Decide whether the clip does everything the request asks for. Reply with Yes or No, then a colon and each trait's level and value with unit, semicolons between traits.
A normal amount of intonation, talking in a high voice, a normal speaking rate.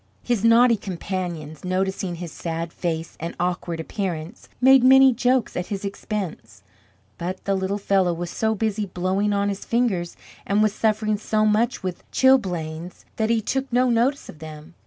Yes: average, 4.3 semitones; high, 195 Hz; average, 165 wpm